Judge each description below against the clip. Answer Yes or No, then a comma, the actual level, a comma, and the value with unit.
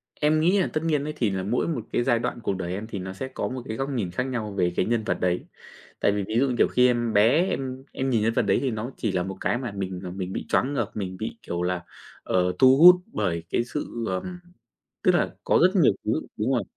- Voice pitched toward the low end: Yes, low, 115 Hz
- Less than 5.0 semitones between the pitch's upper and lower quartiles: No, wide, 5.6 semitones